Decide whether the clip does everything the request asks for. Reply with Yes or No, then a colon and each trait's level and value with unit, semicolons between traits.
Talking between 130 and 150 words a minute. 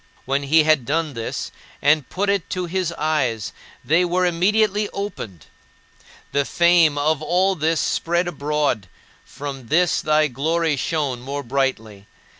Yes: average, 140 wpm